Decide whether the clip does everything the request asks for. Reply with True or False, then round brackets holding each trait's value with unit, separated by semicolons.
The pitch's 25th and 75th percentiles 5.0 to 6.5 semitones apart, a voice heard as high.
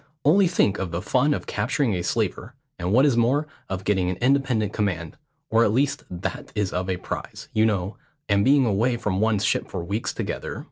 False (5.3 semitones; 105 Hz)